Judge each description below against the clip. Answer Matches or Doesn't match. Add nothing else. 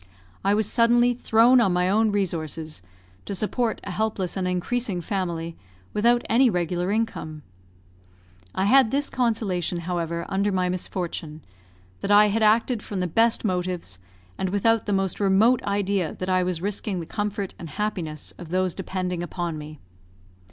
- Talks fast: Doesn't match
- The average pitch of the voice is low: Doesn't match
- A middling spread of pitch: Matches